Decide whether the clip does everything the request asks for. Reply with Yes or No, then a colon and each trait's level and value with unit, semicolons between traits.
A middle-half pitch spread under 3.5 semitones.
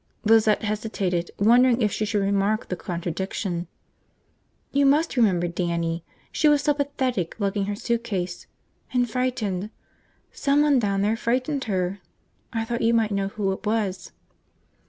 No: average, 4.2 semitones